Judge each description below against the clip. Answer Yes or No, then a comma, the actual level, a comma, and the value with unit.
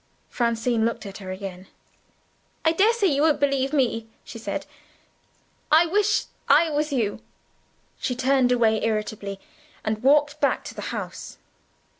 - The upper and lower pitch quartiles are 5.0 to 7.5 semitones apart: Yes, average, 5.3 semitones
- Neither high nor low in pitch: No, very high, 250 Hz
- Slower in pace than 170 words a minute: Yes, average, 140 wpm